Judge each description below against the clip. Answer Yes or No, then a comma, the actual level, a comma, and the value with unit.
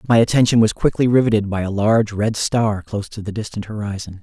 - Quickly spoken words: Yes, fast, 215 wpm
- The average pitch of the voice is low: Yes, low, 105 Hz